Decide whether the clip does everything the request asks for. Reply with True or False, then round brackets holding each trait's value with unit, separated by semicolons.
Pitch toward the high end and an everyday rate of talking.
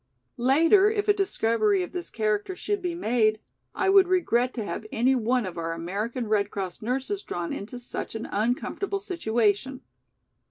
True (245 Hz; 165 wpm)